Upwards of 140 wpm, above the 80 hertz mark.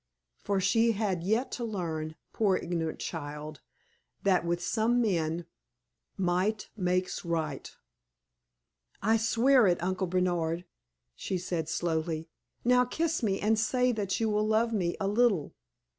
No: slow, 135 wpm; high, 190 Hz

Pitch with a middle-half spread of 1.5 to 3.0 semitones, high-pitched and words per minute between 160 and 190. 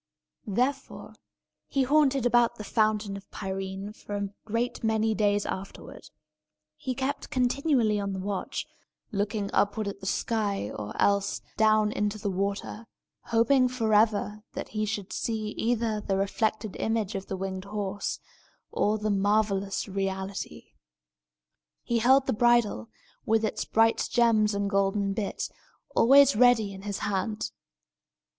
No: narrow, 2.4 semitones; high, 210 Hz; slow, 135 wpm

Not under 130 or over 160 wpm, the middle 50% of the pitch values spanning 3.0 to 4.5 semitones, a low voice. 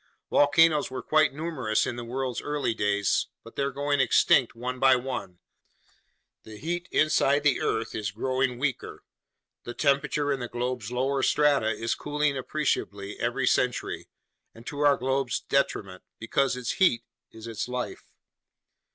Yes: average, 150 wpm; average, 3.7 semitones; low, 130 Hz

